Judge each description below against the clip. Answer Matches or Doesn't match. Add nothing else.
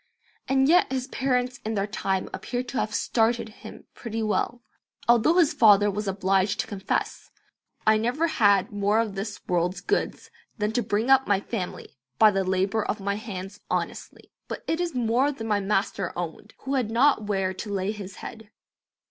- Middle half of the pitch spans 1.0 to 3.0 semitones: Doesn't match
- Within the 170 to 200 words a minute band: Matches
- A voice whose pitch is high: Matches